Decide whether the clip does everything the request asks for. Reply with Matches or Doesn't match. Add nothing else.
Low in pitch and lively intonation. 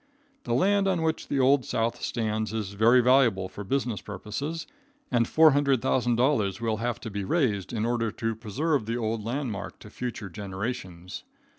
Doesn't match